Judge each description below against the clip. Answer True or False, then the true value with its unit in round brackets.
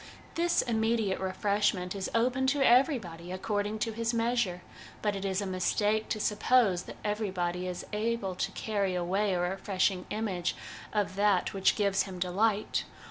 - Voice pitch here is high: True (205 Hz)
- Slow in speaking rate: False (155 wpm)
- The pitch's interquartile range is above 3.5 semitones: False (3.2 semitones)